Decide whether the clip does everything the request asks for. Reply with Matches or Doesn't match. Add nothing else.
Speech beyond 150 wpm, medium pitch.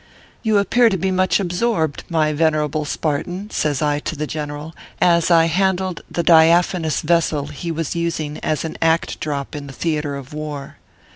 Matches